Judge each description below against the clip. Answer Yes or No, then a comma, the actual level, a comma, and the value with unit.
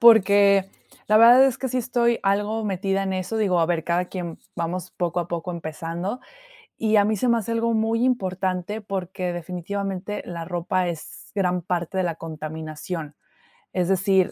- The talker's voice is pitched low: No, medium, 185 Hz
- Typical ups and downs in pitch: Yes, average, 3.5 semitones